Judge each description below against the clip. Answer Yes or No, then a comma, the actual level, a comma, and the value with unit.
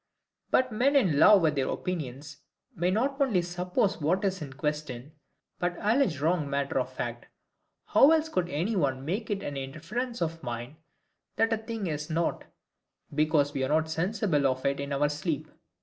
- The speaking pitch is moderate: Yes, medium, 165 Hz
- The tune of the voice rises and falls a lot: Yes, wide, 5.8 semitones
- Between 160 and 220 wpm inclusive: Yes, average, 180 wpm